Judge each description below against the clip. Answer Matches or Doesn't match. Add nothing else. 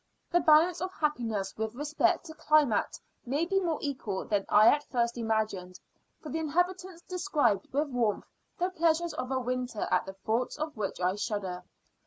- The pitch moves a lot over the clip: Matches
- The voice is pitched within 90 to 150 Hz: Doesn't match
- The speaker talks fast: Doesn't match